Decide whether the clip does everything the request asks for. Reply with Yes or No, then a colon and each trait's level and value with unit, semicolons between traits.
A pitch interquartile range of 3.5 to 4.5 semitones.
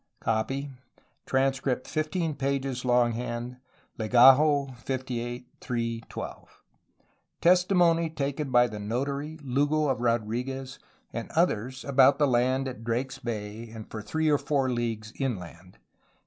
No: average, 2.9 semitones